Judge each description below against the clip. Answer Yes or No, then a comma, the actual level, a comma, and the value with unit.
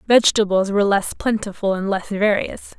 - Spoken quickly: No, average, 150 wpm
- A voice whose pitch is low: No, high, 205 Hz